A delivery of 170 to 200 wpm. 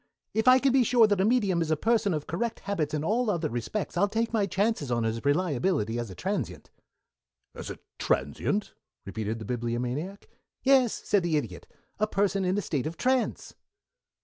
Yes: average, 190 wpm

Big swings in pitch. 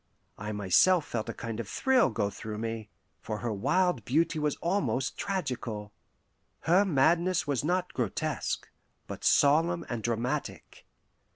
Yes: wide, 7.6 semitones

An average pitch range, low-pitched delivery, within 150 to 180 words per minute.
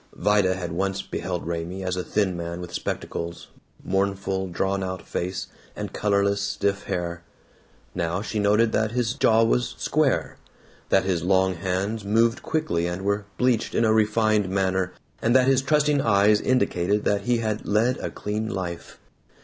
Yes: average, 3.1 semitones; low, 100 Hz; average, 165 wpm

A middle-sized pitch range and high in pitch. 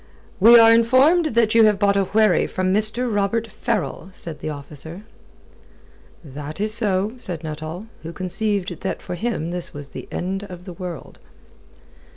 Yes: average, 4.4 semitones; high, 195 Hz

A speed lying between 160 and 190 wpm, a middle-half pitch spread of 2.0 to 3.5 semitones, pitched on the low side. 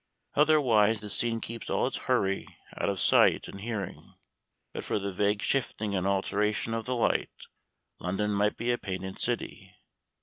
Yes: average, 165 wpm; average, 2.7 semitones; low, 105 Hz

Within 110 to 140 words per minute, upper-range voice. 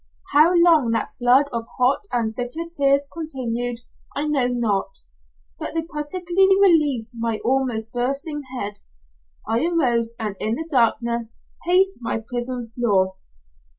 Yes: slow, 135 wpm; high, 245 Hz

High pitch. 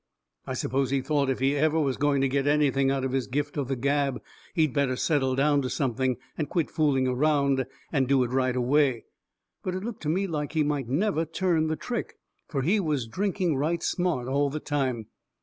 No: medium, 140 Hz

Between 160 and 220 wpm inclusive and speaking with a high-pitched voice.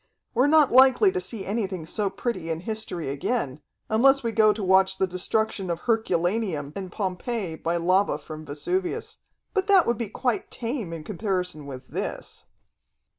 Yes: average, 165 wpm; high, 195 Hz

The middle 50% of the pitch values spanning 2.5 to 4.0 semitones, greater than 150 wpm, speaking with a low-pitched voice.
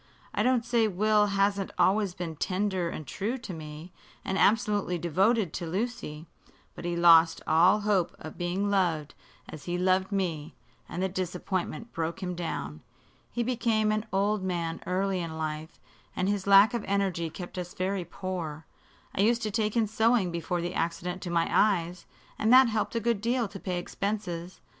No: average, 3.5 semitones; average, 175 wpm; medium, 185 Hz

